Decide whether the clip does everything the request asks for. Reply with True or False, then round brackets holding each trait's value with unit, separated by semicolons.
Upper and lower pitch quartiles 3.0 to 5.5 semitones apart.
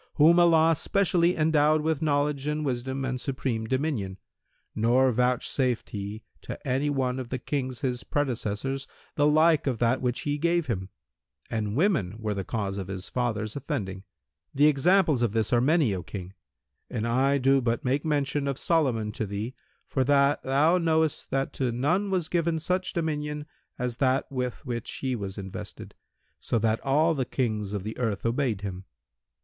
True (4.7 semitones)